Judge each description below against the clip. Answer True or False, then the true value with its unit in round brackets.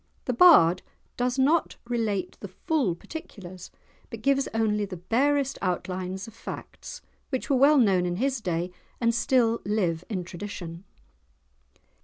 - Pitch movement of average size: False (6.2 semitones)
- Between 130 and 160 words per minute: True (140 wpm)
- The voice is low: False (215 Hz)